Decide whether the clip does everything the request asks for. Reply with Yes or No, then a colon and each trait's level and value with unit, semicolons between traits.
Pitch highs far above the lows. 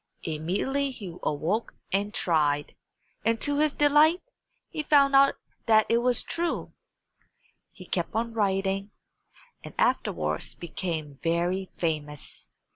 Yes: wide, 8.5 semitones